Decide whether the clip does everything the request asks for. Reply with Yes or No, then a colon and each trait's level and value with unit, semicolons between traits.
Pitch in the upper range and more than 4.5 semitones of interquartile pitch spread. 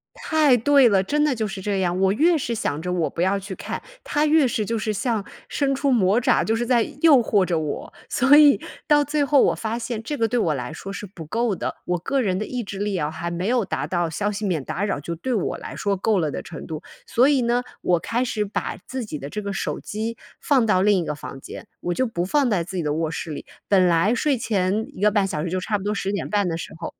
Yes: high, 205 Hz; average, 5.2 semitones